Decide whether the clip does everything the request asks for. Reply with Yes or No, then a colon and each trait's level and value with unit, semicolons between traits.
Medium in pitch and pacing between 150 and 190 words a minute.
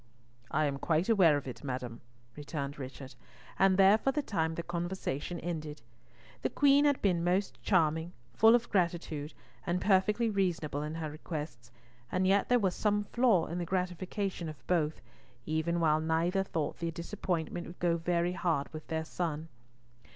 Yes: medium, 170 Hz; average, 165 wpm